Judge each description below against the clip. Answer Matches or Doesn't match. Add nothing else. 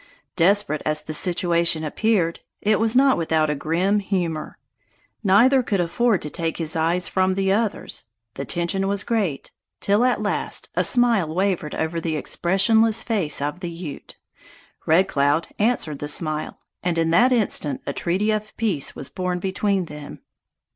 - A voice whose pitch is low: Doesn't match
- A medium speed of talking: Matches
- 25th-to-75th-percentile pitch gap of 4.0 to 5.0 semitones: Matches